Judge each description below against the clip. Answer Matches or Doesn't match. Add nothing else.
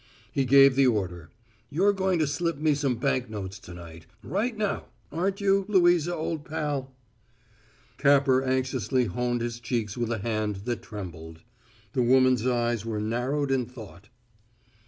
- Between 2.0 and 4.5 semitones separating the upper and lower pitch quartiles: Doesn't match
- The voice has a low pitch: Matches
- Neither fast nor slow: Matches